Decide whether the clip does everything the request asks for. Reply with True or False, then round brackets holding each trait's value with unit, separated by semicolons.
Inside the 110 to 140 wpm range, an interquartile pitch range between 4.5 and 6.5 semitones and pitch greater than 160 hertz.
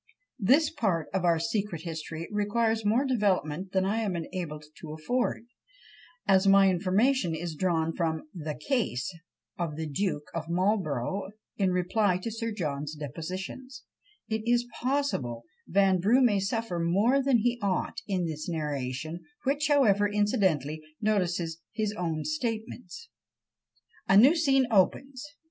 True (135 wpm; 5.5 semitones; 190 Hz)